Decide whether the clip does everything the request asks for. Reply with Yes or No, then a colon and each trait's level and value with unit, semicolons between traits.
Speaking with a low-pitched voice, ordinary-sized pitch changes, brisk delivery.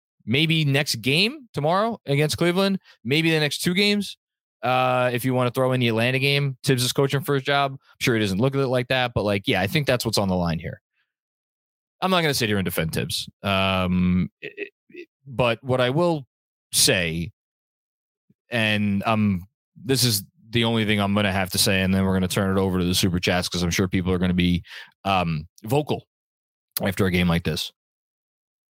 No: low, 125 Hz; wide, 6.5 semitones; fast, 215 wpm